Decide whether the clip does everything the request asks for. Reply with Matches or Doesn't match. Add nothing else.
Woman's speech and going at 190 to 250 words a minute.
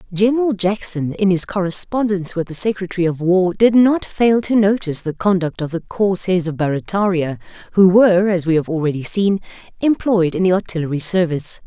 Doesn't match